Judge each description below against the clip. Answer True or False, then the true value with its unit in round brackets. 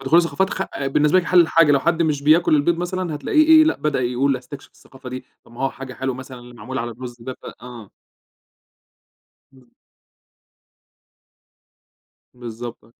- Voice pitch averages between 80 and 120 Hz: False (135 Hz)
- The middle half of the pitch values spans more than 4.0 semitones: True (5.0 semitones)